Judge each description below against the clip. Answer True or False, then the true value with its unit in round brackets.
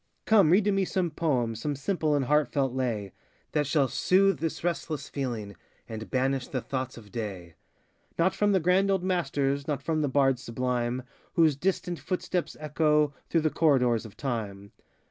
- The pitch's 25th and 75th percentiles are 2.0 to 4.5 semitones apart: False (5.1 semitones)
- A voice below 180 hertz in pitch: True (140 Hz)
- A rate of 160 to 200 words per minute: True (170 wpm)